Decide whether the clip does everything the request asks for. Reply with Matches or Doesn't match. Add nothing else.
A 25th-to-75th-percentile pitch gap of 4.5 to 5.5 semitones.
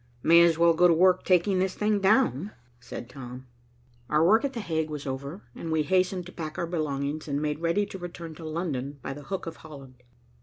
Doesn't match